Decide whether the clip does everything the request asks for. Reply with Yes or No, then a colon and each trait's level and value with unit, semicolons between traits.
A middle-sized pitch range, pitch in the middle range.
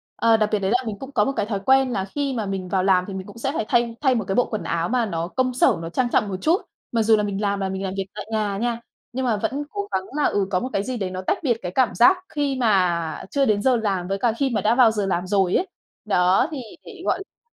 No: average, 4.7 semitones; high, 215 Hz